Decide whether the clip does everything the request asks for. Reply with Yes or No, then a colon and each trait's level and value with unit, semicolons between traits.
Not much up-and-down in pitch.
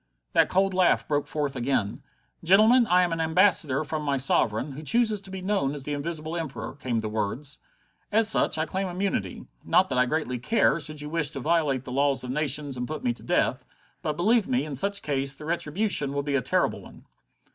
No: average, 4.9 semitones